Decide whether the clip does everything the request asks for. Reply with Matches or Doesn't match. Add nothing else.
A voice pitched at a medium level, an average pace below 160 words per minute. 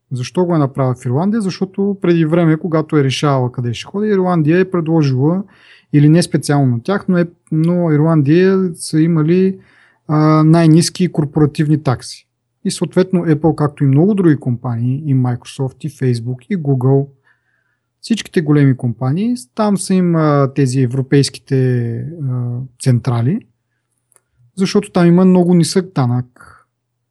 Matches